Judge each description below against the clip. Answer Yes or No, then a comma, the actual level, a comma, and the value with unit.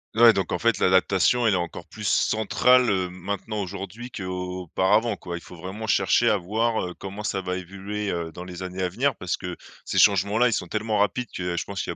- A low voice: Yes, very low, 95 Hz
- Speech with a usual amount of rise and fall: Yes, average, 3.1 semitones